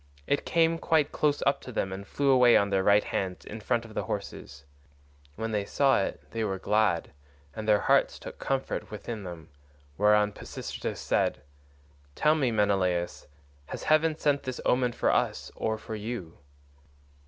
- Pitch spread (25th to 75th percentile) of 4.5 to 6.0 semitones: Yes, average, 5.1 semitones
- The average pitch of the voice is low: Yes, low, 110 Hz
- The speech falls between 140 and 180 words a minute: Yes, average, 170 wpm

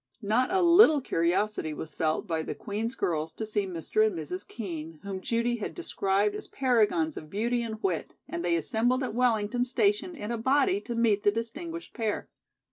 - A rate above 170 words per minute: Yes, average, 190 wpm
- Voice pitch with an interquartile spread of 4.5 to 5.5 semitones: Yes, average, 4.9 semitones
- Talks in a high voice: Yes, high, 220 Hz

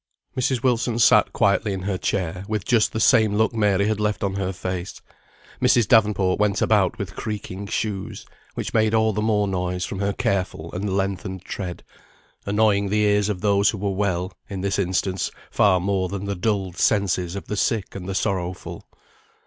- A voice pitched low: Yes, low, 100 Hz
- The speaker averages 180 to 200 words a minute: Yes, average, 185 wpm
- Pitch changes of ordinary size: No, narrow, 2.1 semitones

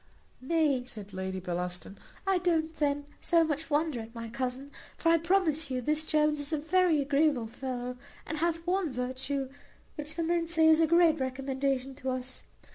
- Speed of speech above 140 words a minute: Yes, average, 180 wpm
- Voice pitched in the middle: No, very high, 290 Hz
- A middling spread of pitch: Yes, average, 4.1 semitones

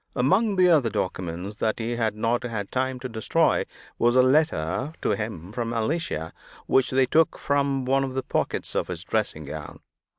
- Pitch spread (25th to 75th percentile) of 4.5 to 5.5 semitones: No, average, 4.1 semitones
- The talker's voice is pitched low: Yes, low, 125 Hz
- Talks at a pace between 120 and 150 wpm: No, average, 185 wpm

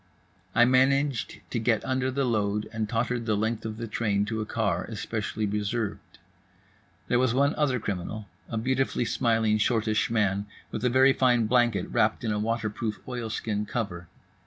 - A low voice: Yes, low, 115 Hz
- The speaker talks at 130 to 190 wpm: Yes, average, 170 wpm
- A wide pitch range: No, average, 2.7 semitones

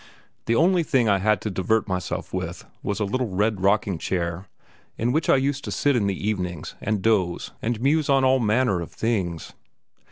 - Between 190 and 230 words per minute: Yes, average, 195 wpm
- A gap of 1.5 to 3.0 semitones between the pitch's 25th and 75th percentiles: No, wide, 5.4 semitones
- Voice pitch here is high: No, low, 105 Hz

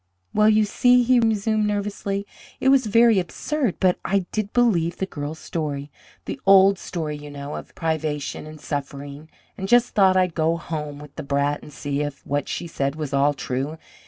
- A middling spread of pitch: No, wide, 6.0 semitones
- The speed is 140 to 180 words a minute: No, average, 190 wpm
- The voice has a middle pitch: Yes, medium, 165 Hz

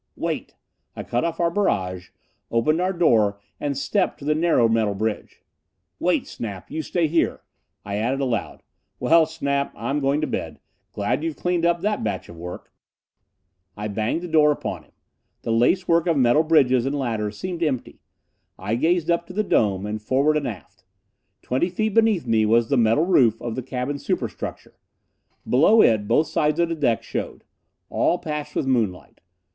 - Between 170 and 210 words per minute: Yes, average, 175 wpm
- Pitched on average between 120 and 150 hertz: Yes, medium, 140 Hz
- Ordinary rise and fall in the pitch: No, wide, 6.6 semitones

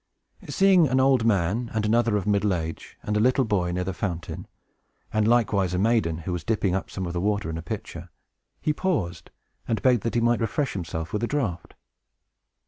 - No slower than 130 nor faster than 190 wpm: No, fast, 205 wpm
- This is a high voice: No, low, 105 Hz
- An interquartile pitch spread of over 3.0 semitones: Yes, average, 4.8 semitones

